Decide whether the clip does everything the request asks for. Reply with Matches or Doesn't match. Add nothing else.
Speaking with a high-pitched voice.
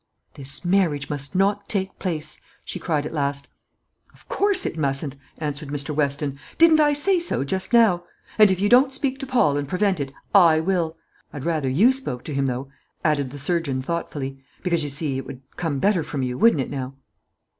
Doesn't match